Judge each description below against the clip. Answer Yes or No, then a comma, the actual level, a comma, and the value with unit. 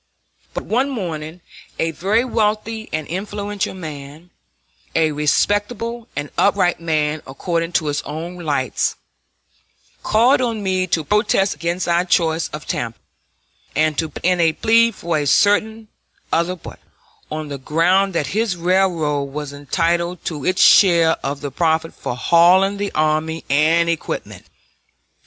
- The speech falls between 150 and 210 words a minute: No, average, 140 wpm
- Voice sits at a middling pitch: Yes, medium, 170 Hz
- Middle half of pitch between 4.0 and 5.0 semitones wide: Yes, average, 4.3 semitones